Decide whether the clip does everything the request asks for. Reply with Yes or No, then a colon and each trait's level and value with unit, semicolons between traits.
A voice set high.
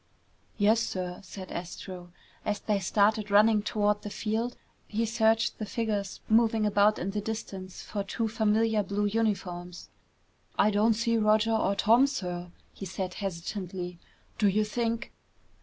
Yes: high, 210 Hz